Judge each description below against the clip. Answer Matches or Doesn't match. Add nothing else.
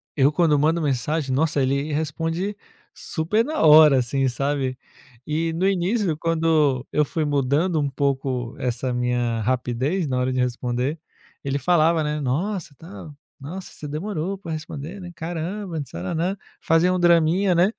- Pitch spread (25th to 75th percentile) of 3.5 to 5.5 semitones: Matches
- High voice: Doesn't match